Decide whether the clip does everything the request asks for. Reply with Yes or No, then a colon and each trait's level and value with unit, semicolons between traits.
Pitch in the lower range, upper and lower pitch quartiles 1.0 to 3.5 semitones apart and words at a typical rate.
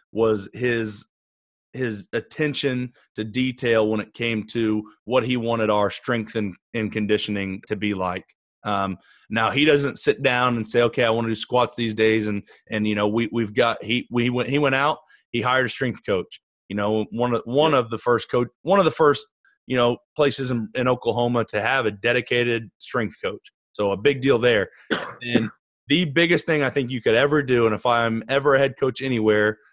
No: low, 115 Hz; average, 3.0 semitones; fast, 210 wpm